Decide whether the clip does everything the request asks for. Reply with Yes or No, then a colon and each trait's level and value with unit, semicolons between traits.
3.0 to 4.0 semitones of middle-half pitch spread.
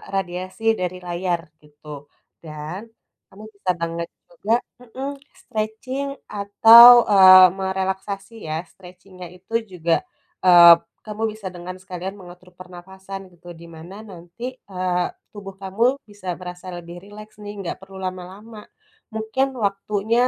No: narrow, 2.5 semitones